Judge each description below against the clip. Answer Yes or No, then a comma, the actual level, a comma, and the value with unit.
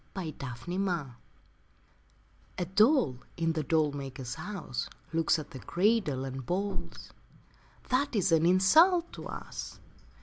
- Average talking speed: No, slow, 130 wpm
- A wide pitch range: Yes, wide, 6.2 semitones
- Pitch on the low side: No, medium, 170 Hz